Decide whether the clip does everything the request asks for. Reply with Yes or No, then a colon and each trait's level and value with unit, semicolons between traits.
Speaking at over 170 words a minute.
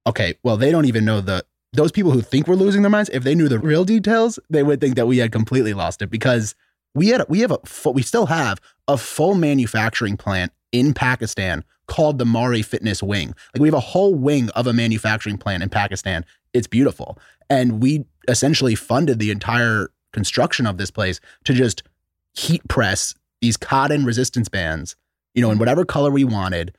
Yes: average, 200 wpm